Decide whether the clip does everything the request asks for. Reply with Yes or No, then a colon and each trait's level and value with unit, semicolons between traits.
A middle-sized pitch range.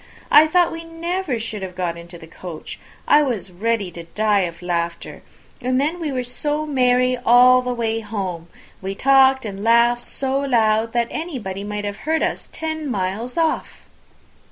No: wide, 5.8 semitones